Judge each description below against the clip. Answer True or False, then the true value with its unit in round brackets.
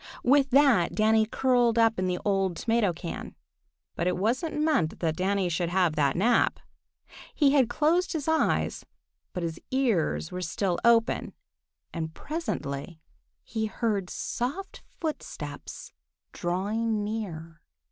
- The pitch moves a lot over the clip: True (6.2 semitones)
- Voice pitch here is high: True (215 Hz)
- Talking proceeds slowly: True (130 wpm)